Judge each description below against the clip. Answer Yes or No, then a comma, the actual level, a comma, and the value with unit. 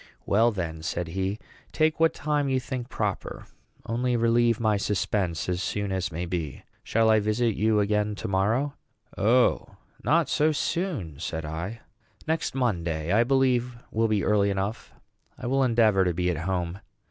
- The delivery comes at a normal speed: Yes, average, 165 wpm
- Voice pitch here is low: Yes, low, 105 Hz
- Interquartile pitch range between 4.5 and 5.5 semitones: Yes, average, 5.1 semitones